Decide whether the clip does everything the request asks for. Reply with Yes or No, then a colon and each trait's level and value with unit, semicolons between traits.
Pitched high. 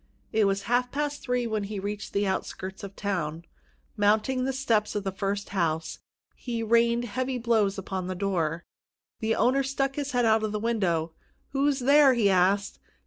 Yes: high, 215 Hz